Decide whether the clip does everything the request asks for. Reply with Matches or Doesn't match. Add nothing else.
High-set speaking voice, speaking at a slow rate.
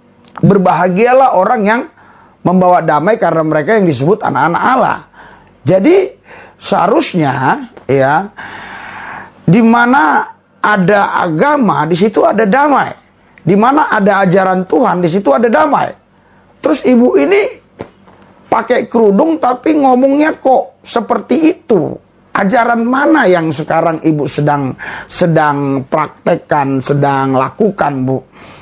Matches